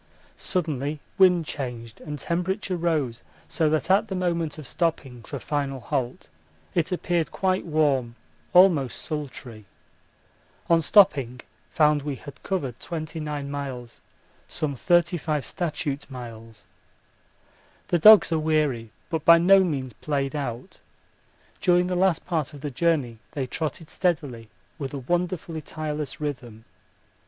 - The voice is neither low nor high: Yes, medium, 150 Hz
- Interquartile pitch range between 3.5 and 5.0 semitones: Yes, average, 4.3 semitones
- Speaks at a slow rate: Yes, slow, 130 wpm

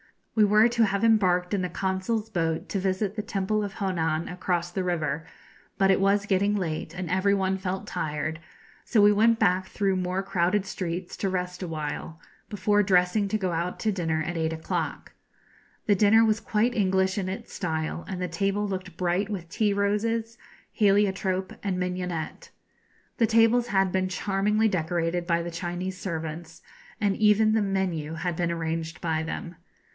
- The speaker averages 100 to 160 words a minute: No, average, 175 wpm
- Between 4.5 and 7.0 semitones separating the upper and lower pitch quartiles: No, average, 3.0 semitones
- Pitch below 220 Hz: Yes, high, 190 Hz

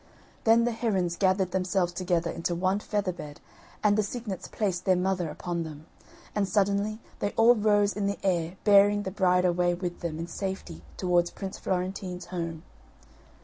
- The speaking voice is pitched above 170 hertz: Yes, medium, 185 Hz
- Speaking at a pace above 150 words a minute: Yes, average, 170 wpm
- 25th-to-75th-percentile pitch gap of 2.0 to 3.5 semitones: Yes, narrow, 2.6 semitones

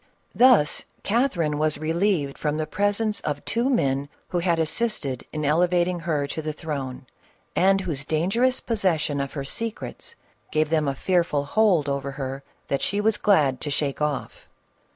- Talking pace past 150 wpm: Yes, average, 160 wpm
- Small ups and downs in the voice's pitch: No, wide, 5.5 semitones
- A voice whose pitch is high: No, medium, 155 Hz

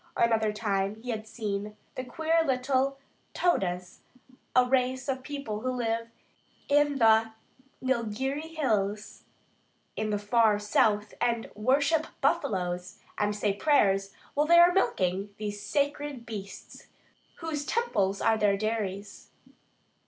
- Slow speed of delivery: Yes, slow, 125 wpm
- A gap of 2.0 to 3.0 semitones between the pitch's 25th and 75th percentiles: No, average, 4.9 semitones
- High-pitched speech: Yes, high, 225 Hz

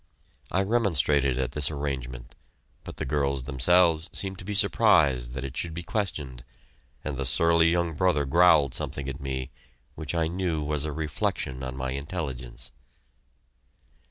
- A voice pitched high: No, very low, 75 Hz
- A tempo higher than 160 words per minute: No, average, 155 wpm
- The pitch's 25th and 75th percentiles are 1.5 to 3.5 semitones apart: No, average, 4.5 semitones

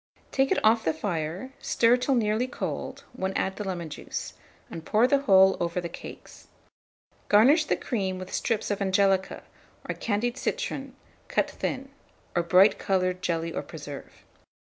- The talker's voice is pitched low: No, high, 195 Hz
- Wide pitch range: No, average, 5.0 semitones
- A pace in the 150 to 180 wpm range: Yes, average, 160 wpm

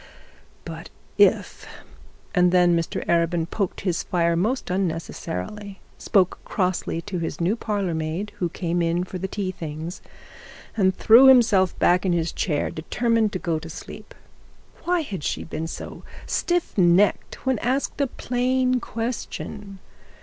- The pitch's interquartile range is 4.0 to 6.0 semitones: Yes, average, 4.5 semitones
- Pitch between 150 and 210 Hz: Yes, medium, 185 Hz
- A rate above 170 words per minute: No, average, 145 wpm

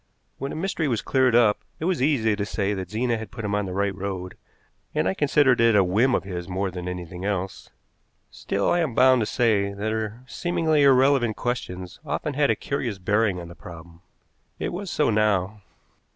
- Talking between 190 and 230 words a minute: Yes, fast, 205 wpm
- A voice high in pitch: No, low, 110 Hz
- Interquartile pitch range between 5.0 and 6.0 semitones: Yes, wide, 5.4 semitones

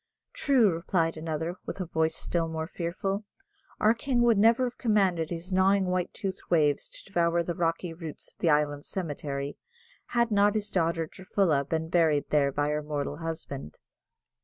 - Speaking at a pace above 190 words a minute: No, average, 170 wpm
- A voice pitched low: No, medium, 170 Hz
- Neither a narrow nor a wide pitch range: Yes, average, 3.8 semitones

